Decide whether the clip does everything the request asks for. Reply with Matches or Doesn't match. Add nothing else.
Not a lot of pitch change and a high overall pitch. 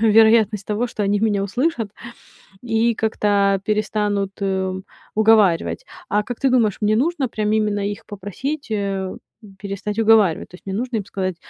Matches